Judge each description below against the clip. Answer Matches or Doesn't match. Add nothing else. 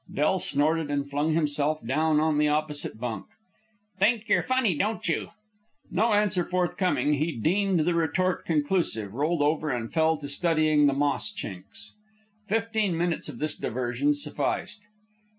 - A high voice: Doesn't match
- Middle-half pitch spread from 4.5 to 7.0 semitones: Doesn't match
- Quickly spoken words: Doesn't match